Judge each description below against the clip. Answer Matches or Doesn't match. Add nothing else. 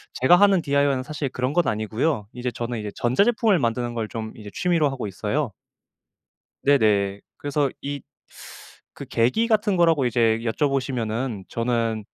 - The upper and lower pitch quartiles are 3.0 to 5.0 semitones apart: Matches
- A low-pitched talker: Matches